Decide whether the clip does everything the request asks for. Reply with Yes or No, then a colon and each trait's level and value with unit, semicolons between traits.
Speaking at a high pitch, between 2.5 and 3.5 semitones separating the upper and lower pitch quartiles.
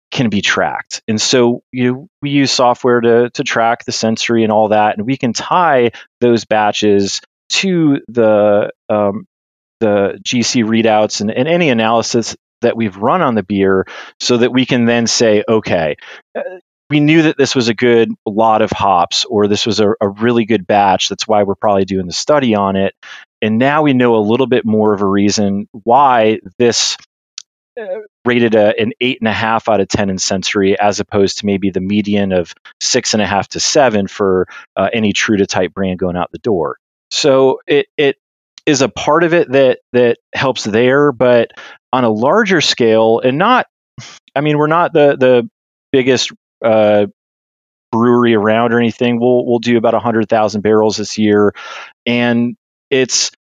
No: low, 115 Hz; average, 3.2 semitones